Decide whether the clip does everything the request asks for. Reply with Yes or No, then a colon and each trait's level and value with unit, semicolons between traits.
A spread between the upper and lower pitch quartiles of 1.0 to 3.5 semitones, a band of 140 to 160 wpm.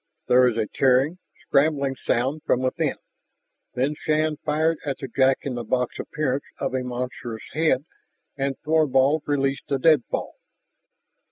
Yes: average, 2.9 semitones; average, 145 wpm